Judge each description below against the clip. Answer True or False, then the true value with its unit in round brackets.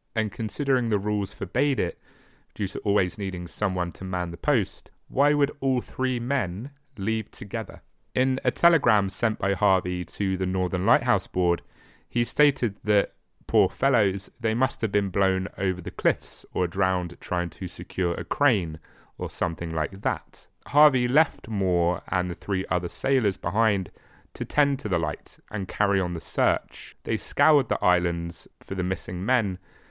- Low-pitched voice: True (100 Hz)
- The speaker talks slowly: False (170 wpm)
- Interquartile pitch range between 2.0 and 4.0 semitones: False (4.6 semitones)